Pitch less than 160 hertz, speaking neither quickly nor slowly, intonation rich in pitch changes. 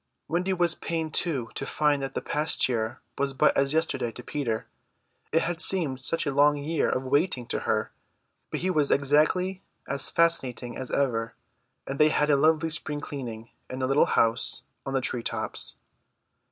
No: medium, 140 Hz; average, 180 wpm; average, 3.7 semitones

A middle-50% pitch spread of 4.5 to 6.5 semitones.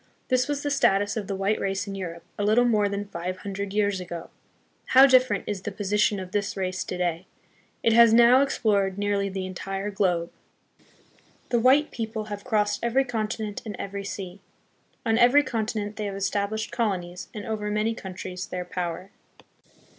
No: narrow, 2.6 semitones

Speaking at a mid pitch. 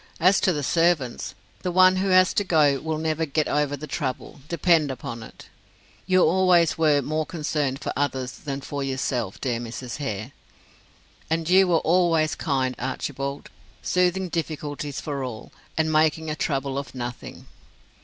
Yes: medium, 150 Hz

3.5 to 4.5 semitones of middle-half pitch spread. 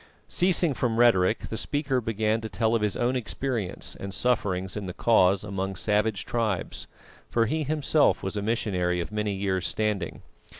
Yes: average, 3.8 semitones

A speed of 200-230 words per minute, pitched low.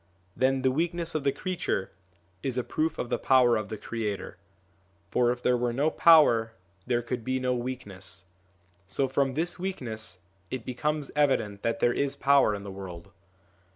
No: average, 175 wpm; low, 125 Hz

